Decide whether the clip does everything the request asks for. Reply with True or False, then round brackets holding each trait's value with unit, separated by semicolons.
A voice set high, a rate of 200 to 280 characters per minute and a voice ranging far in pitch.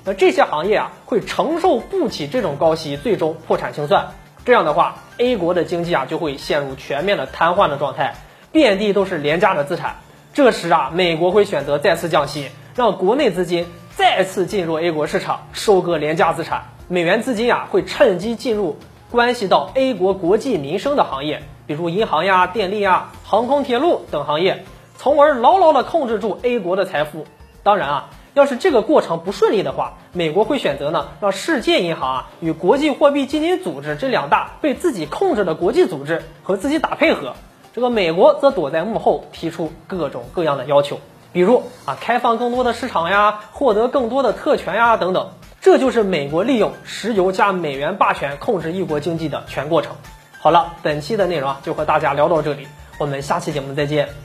False (195 Hz; 305 characters per minute; 7.4 semitones)